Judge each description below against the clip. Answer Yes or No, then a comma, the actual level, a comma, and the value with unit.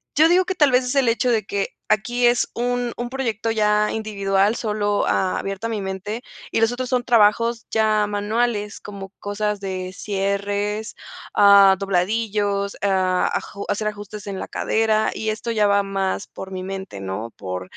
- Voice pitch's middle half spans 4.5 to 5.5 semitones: No, narrow, 2.5 semitones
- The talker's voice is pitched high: Yes, high, 210 Hz